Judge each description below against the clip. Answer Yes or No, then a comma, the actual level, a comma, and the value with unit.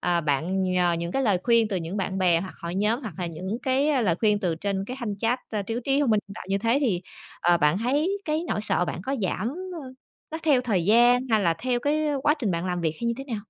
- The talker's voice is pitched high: Yes, high, 210 Hz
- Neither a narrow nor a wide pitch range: No, wide, 6.2 semitones